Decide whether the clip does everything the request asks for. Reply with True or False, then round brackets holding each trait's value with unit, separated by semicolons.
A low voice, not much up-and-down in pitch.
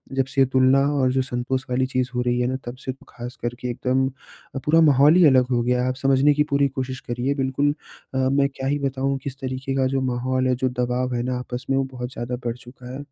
True (130 Hz; 1.4 semitones)